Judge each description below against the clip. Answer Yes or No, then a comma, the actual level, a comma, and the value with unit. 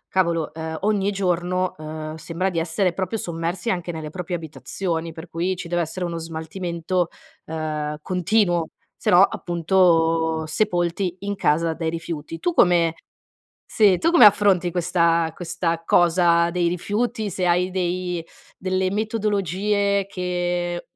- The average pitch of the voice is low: No, medium, 175 Hz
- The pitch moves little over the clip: Yes, narrow, 2.3 semitones